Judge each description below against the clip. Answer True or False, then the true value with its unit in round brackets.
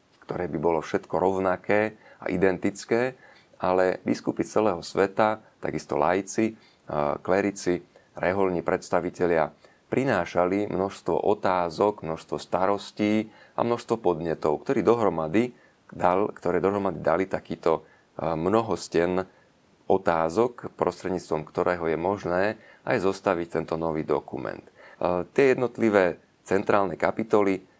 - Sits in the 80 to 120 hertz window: True (95 Hz)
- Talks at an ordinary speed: False (100 wpm)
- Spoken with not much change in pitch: False (3.3 semitones)